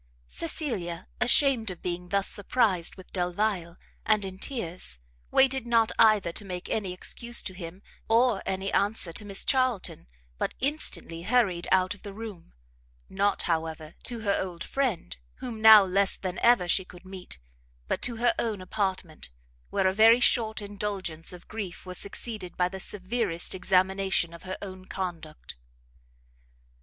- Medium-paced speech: Yes, average, 155 wpm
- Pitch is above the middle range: Yes, high, 195 Hz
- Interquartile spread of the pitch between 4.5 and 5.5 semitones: No, average, 3.7 semitones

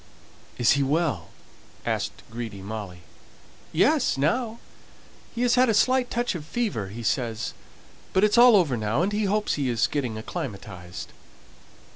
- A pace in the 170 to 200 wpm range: No, average, 150 wpm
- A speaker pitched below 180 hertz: Yes, medium, 140 Hz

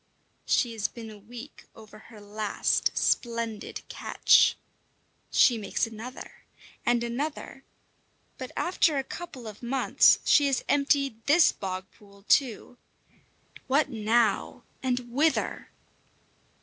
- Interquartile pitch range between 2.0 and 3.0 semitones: No, average, 3.9 semitones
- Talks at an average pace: No, slow, 115 wpm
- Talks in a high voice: Yes, high, 235 Hz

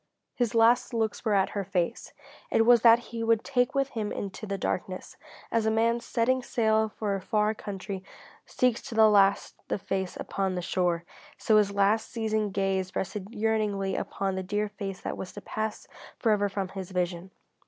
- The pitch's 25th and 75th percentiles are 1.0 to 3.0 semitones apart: Yes, average, 2.7 semitones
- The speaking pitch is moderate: No, high, 210 Hz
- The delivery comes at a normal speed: Yes, average, 185 wpm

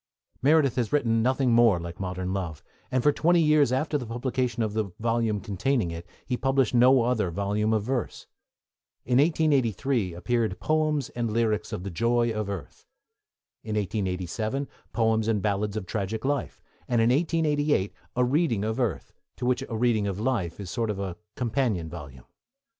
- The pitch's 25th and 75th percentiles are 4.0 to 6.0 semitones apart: Yes, average, 4.4 semitones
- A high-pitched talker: No, low, 115 Hz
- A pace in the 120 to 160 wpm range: No, average, 170 wpm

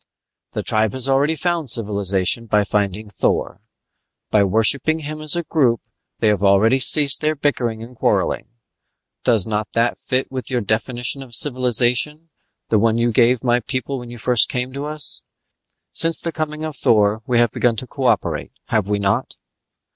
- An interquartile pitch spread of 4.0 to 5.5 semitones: Yes, average, 4.3 semitones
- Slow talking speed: No, average, 175 wpm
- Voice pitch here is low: Yes, low, 120 Hz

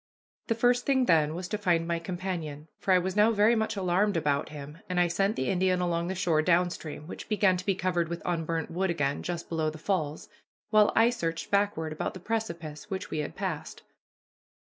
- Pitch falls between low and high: Yes, medium, 175 Hz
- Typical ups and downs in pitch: Yes, average, 3.6 semitones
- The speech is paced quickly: Yes, fast, 215 wpm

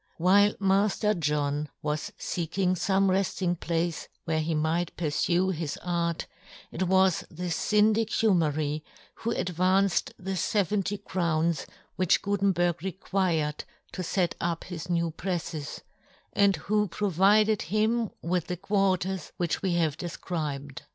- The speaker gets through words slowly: Yes, slow, 130 wpm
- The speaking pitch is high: No, medium, 180 Hz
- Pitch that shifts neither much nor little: Yes, average, 3.1 semitones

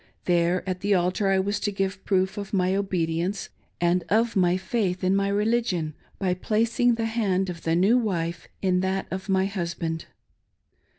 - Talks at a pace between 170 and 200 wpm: Yes, average, 175 wpm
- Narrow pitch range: Yes, narrow, 2.2 semitones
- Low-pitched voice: No, high, 190 Hz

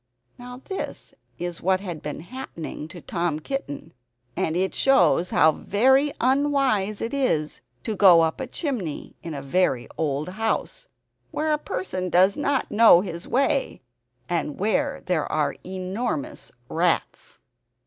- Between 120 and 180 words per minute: Yes, average, 140 wpm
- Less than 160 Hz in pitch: No, medium, 185 Hz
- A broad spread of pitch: Yes, wide, 7.7 semitones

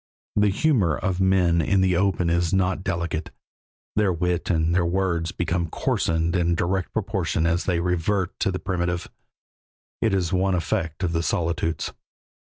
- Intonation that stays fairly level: Yes, narrow, 2.1 semitones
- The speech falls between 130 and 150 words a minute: No, average, 160 wpm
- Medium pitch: No, very low, 90 Hz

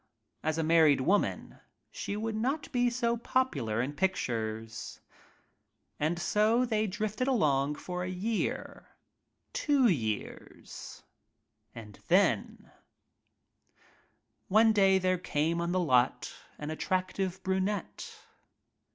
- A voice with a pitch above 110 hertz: Yes, medium, 185 Hz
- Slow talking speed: Yes, slow, 115 wpm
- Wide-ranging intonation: Yes, wide, 6.6 semitones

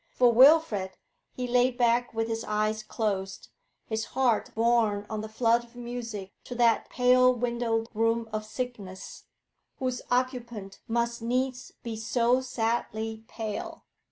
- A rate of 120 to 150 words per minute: Yes, slow, 135 wpm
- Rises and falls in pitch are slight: Yes, narrow, 2.1 semitones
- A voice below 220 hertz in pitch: No, high, 235 Hz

